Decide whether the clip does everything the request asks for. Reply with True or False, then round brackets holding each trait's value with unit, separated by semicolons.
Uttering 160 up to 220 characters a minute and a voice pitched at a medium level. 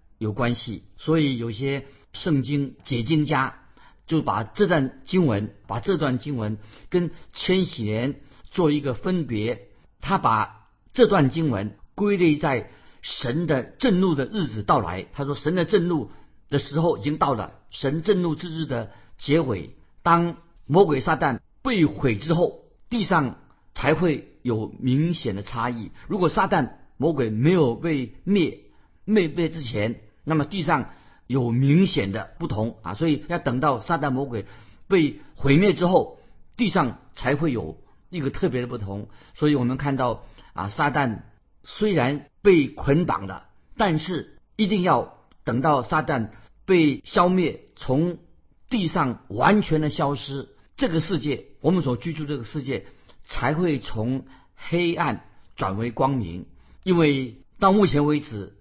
True (210 characters per minute; 145 Hz)